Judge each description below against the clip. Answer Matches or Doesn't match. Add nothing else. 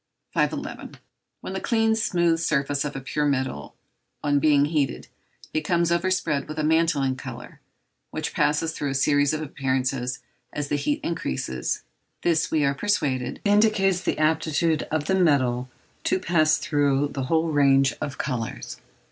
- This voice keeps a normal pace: Matches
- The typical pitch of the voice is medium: Matches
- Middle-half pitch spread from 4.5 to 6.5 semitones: Doesn't match